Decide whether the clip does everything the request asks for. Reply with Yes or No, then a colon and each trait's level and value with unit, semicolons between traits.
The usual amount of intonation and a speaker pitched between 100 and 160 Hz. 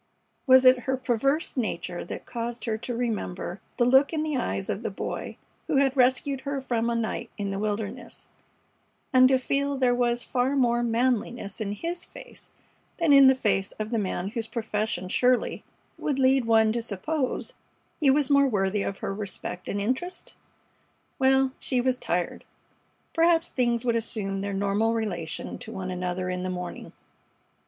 No: average, 4.4 semitones; high, 235 Hz